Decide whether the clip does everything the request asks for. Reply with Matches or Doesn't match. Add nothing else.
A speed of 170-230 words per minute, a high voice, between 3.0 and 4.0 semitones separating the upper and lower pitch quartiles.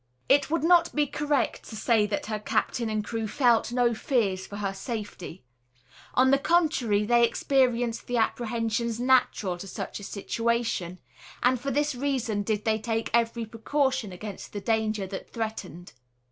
Doesn't match